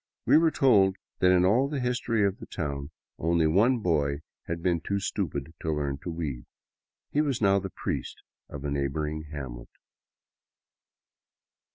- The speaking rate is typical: Yes, average, 160 wpm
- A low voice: Yes, very low, 85 Hz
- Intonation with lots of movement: Yes, wide, 5.7 semitones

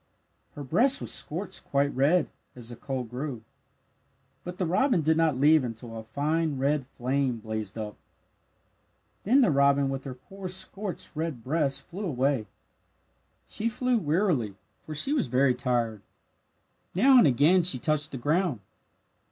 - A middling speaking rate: Yes, average, 150 wpm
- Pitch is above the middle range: No, medium, 145 Hz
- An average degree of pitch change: No, wide, 5.9 semitones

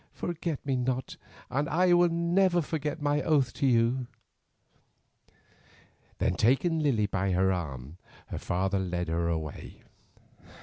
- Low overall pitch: Yes, low, 130 Hz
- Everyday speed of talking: No, slow, 130 wpm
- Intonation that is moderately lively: No, wide, 9.0 semitones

